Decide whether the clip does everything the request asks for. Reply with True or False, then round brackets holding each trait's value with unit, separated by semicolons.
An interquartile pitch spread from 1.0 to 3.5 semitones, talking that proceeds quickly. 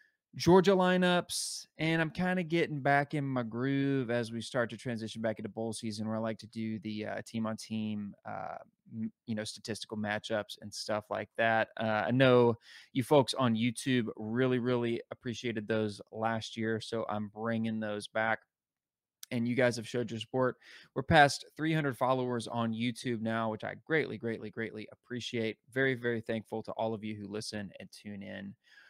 False (2.8 semitones; 180 wpm)